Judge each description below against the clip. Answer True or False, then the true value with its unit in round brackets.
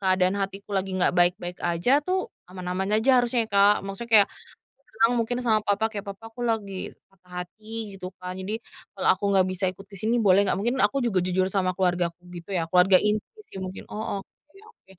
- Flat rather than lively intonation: False (3.1 semitones)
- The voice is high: True (195 Hz)